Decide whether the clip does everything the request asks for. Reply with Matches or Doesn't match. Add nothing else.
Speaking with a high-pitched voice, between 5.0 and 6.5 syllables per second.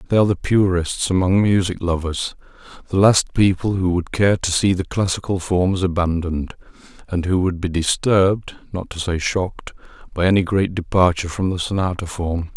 Doesn't match